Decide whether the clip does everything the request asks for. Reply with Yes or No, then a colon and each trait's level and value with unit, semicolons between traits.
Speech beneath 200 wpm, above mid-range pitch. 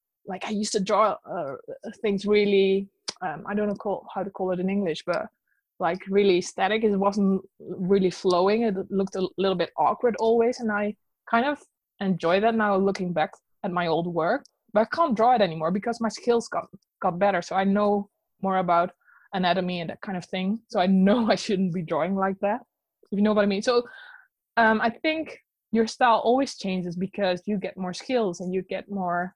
No: fast, 205 wpm; high, 200 Hz